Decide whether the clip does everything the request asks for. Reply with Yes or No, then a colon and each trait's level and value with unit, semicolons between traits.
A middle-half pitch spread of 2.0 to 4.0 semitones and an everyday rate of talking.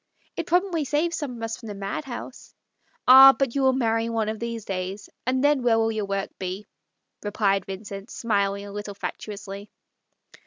No: average, 4.6 semitones; average, 190 wpm